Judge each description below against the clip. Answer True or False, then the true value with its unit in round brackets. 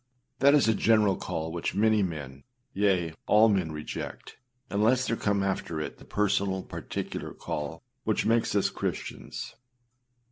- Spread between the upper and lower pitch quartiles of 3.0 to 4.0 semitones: False (4.7 semitones)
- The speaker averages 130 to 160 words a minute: True (150 wpm)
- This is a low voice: True (100 Hz)